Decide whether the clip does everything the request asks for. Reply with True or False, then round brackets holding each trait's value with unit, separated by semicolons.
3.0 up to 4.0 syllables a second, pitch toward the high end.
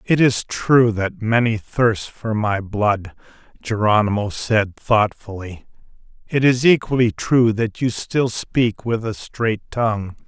False (3.7 syllables/s; 115 Hz)